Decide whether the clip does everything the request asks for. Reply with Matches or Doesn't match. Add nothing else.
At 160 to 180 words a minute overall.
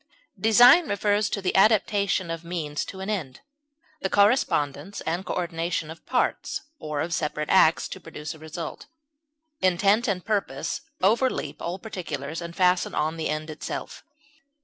Doesn't match